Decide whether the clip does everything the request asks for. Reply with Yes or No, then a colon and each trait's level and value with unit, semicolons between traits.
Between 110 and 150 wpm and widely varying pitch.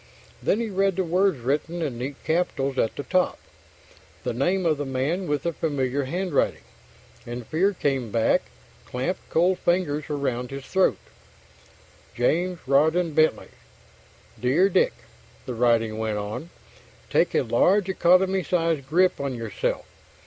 Yes: average, 140 wpm; wide, 5.7 semitones